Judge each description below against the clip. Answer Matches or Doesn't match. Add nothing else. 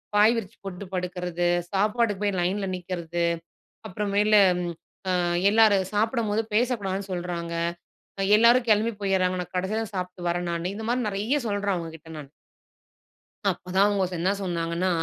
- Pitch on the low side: Doesn't match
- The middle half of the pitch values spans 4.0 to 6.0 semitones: Doesn't match